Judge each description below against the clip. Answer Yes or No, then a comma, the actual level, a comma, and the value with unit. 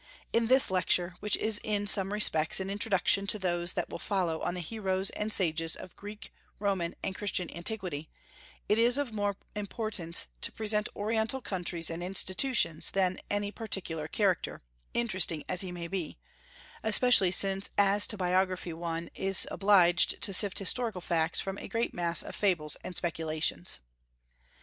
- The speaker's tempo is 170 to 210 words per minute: No, average, 160 wpm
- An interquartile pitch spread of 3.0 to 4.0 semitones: Yes, average, 3.3 semitones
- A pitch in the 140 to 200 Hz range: Yes, high, 190 Hz